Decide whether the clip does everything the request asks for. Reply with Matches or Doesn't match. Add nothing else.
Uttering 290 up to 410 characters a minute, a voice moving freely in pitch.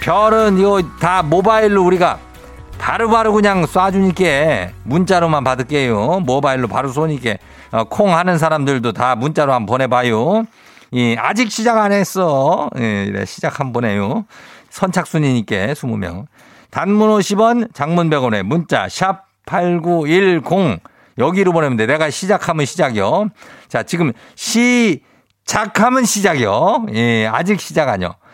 Doesn't match